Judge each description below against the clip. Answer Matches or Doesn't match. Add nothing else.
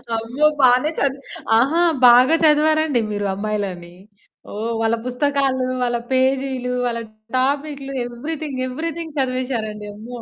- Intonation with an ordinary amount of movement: Matches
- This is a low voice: Doesn't match